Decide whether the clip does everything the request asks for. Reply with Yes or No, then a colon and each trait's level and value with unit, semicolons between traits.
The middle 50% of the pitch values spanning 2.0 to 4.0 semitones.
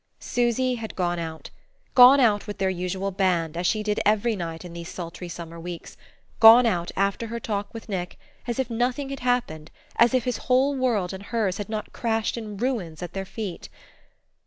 No: average, 5.0 semitones